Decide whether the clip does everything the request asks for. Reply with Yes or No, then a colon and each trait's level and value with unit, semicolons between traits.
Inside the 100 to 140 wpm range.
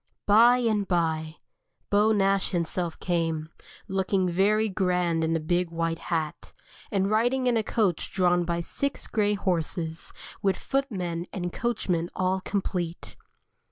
Yes: slow, 135 wpm